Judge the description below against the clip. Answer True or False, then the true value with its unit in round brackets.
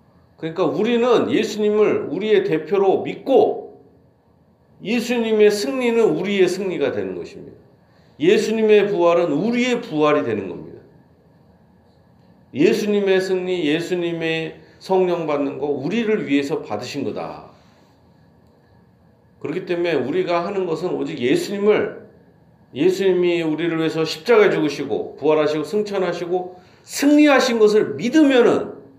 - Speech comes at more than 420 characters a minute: False (285 characters per minute)